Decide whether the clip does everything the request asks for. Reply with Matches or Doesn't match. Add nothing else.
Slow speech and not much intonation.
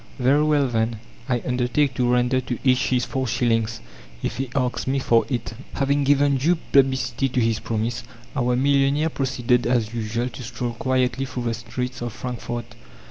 Doesn't match